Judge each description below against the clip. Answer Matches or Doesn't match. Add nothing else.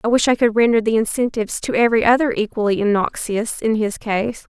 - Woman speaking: Matches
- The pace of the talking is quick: Doesn't match